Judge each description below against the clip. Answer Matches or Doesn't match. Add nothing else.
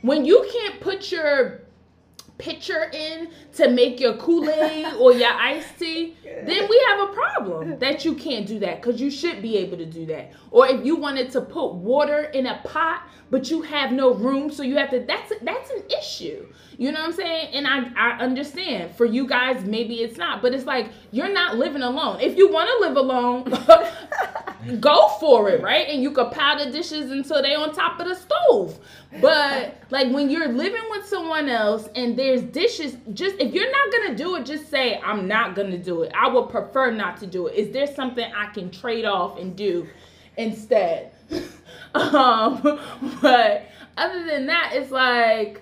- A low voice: Doesn't match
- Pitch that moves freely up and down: Doesn't match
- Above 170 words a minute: Matches